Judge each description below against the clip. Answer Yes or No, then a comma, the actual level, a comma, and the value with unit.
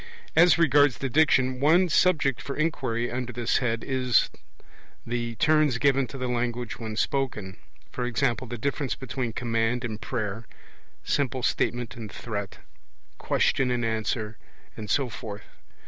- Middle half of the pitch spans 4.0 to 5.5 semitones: No, average, 3.1 semitones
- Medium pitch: No, low, 125 Hz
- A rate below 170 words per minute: Yes, average, 140 wpm